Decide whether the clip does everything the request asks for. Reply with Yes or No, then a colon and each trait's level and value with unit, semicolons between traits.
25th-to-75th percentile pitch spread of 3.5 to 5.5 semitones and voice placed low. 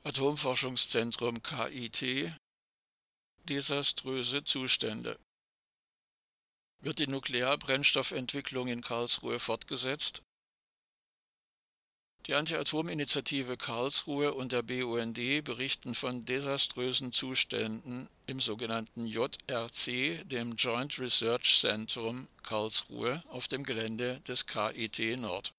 No: narrow, 2.6 semitones; low, 125 Hz